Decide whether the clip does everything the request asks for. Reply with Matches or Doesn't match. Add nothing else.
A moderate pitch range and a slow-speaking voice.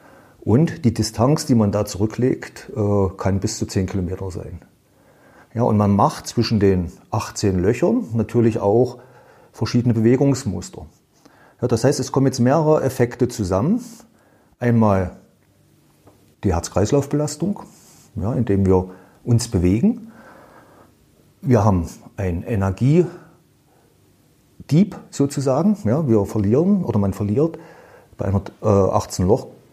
Doesn't match